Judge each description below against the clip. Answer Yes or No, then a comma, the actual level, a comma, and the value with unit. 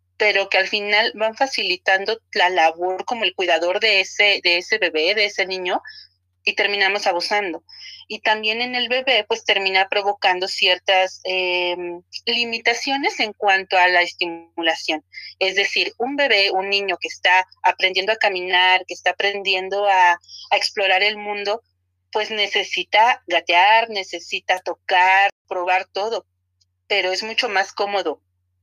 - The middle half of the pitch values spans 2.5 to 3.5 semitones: Yes, average, 2.8 semitones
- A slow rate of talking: No, average, 145 wpm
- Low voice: No, high, 190 Hz